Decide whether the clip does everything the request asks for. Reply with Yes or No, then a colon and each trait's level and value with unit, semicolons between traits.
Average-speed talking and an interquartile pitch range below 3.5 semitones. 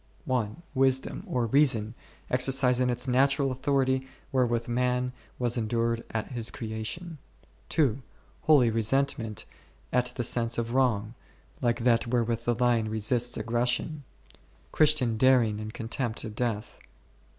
No: slow, 130 wpm; narrow, 2.4 semitones